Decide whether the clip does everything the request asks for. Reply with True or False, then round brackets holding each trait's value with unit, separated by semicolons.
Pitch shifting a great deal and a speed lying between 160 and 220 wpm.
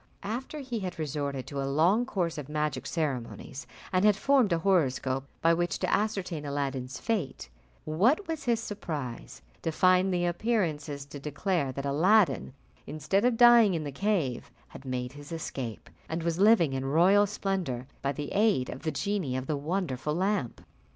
True (6.3 semitones; 170 wpm)